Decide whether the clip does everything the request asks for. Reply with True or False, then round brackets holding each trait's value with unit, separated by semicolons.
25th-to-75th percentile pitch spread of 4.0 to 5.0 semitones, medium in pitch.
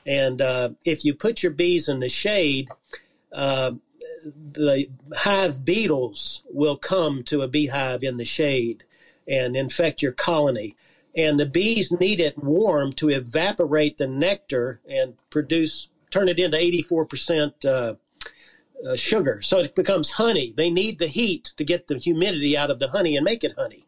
True (4.3 semitones; 155 Hz)